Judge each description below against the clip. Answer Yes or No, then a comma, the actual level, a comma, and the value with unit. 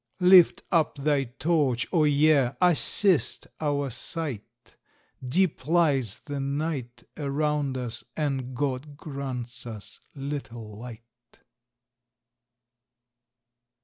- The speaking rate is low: Yes, slow, 90 wpm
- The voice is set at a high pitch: No, medium, 140 Hz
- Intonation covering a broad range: No, average, 3.6 semitones